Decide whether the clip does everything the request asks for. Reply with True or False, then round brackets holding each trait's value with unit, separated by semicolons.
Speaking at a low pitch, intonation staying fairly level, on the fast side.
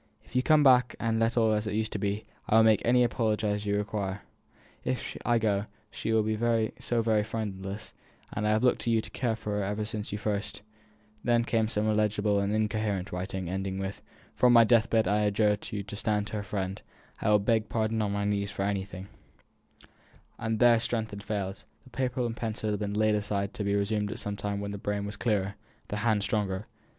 True (105 Hz; 1.7 semitones; 225 wpm)